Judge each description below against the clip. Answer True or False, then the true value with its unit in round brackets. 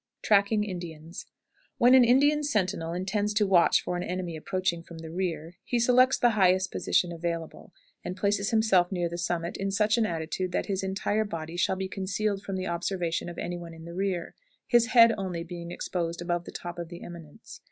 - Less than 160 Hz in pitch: False (185 Hz)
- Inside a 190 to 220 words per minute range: True (200 wpm)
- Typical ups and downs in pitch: True (3.3 semitones)